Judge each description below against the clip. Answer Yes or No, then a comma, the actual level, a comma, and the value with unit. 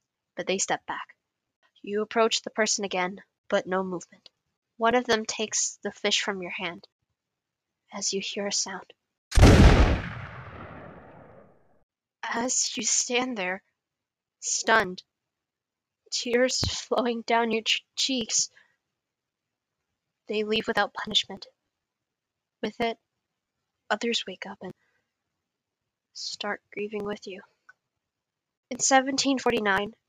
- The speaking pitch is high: Yes, high, 215 Hz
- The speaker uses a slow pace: Yes, slow, 105 wpm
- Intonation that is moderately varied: Yes, average, 3.1 semitones